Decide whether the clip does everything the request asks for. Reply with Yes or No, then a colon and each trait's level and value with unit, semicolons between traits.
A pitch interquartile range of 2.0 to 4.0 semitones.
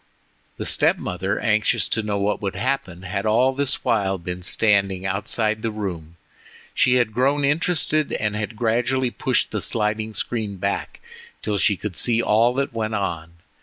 Yes: average, 3.7 semitones